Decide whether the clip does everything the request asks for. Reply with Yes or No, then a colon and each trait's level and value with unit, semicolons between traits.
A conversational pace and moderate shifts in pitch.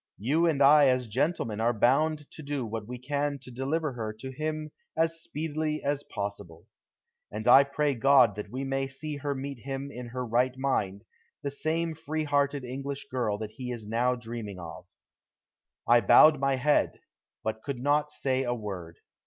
Yes: average, 180 wpm; average, 3.7 semitones